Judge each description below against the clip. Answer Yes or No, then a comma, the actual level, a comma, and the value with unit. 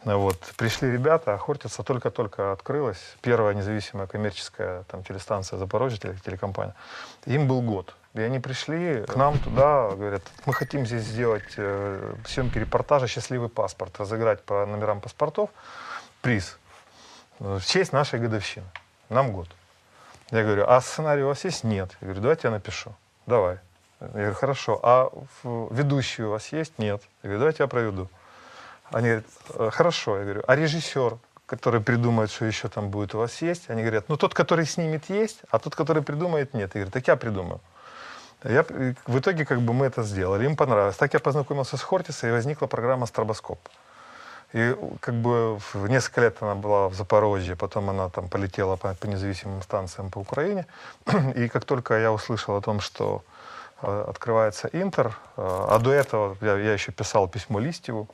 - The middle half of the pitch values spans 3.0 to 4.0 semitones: No, average, 5.1 semitones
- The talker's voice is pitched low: Yes, low, 115 Hz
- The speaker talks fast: Yes, fast, 165 wpm